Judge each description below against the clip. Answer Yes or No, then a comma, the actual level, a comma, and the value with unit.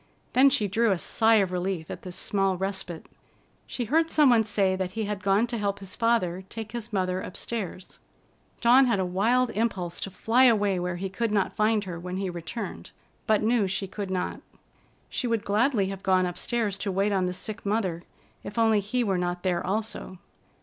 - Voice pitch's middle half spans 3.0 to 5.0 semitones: Yes, average, 3.4 semitones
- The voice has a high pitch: Yes, high, 200 Hz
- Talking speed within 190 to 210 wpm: Yes, average, 200 wpm